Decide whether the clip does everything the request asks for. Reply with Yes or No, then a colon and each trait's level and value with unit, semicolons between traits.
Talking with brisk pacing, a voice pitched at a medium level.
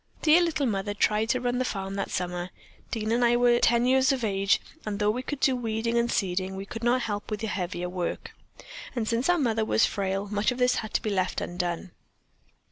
No: fast, 225 wpm; high, 220 Hz